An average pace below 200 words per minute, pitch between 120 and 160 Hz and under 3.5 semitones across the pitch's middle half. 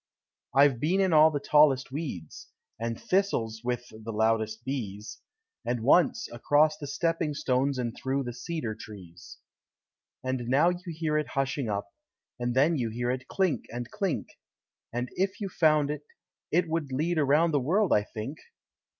No: average, 165 wpm; low, 135 Hz; average, 4.9 semitones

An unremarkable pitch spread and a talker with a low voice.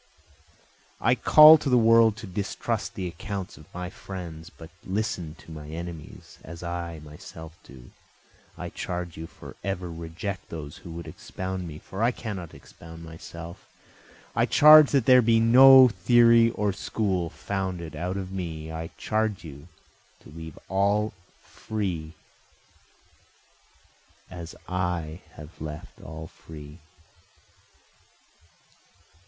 Yes: average, 4.8 semitones; very low, 90 Hz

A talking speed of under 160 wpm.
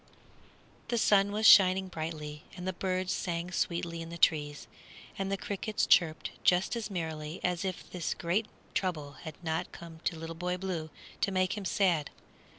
No: average, 170 wpm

